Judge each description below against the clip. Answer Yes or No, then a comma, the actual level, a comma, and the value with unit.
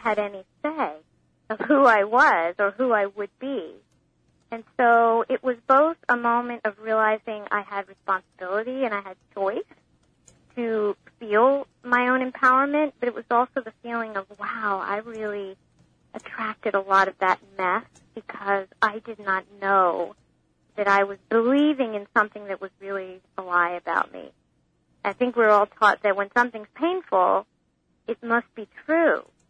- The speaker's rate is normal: Yes, average, 165 wpm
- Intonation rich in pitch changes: No, average, 3.5 semitones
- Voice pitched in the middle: No, high, 215 Hz